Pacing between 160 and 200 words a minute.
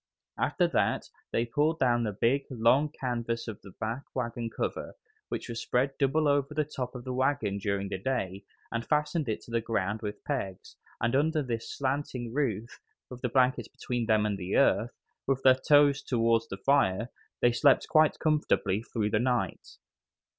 Yes: average, 180 wpm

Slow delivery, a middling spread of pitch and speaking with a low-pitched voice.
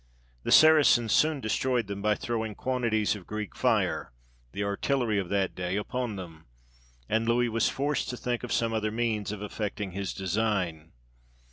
No: average, 165 wpm; average, 3.2 semitones; low, 110 Hz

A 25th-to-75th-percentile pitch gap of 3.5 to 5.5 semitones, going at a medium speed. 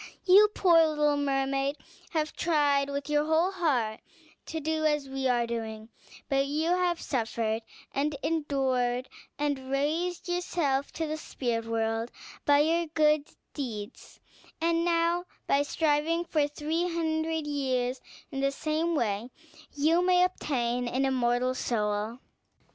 No: average, 4.1 semitones; slow, 130 wpm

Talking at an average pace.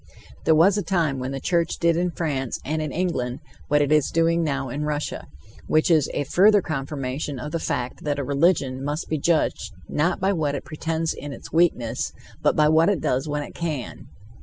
No: fast, 210 wpm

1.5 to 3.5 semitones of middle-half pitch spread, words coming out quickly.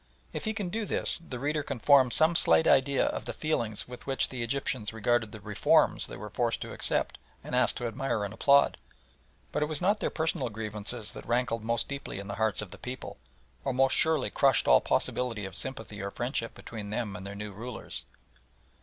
No: average, 4.6 semitones; fast, 210 wpm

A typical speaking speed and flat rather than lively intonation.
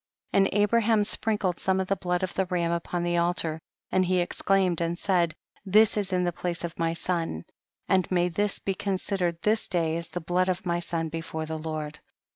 No: fast, 215 wpm; narrow, 2.2 semitones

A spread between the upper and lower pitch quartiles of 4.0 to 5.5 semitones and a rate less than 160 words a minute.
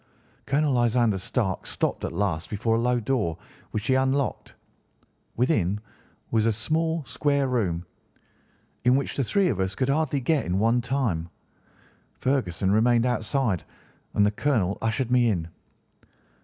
Yes: average, 4.7 semitones; average, 145 wpm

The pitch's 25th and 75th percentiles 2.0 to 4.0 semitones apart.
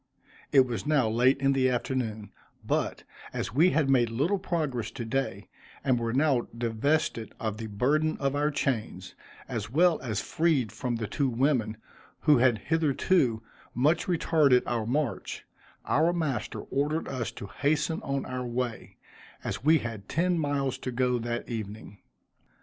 No: average, 4.5 semitones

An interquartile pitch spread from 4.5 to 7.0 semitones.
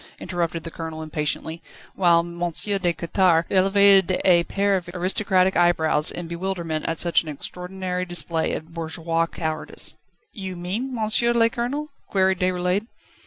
No: narrow, 2.5 semitones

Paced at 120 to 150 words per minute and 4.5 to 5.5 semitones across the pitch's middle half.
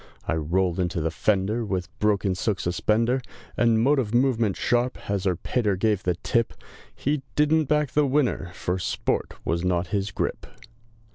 No: average, 160 wpm; average, 5.2 semitones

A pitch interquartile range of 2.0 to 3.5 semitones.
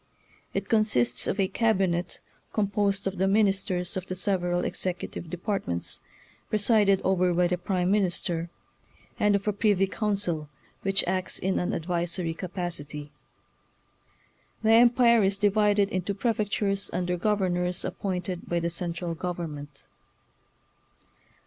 Yes: narrow, 2.5 semitones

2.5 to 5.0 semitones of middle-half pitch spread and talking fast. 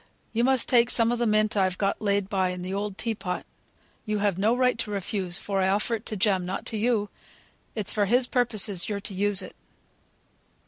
Yes: average, 2.9 semitones; fast, 220 wpm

